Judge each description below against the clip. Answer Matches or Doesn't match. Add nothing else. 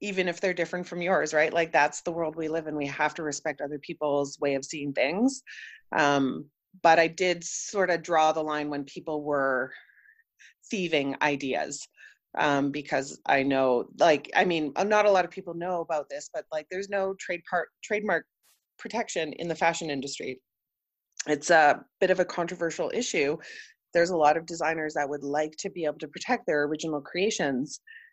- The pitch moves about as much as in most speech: Matches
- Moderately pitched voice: Matches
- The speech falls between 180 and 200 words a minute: Matches